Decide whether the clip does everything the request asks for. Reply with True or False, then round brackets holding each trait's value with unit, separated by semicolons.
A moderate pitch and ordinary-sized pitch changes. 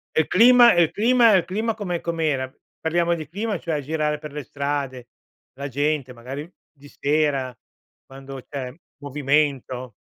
True (150 Hz; 4.0 semitones)